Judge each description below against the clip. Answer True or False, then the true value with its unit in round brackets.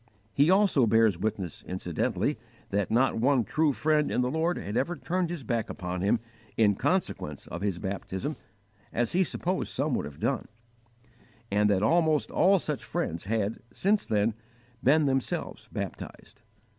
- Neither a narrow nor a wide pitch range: False (7.5 semitones)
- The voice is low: True (120 Hz)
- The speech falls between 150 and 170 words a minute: True (155 wpm)